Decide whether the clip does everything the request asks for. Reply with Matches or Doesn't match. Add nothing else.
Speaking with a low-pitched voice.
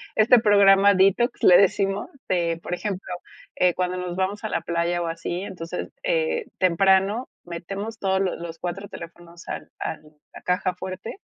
Doesn't match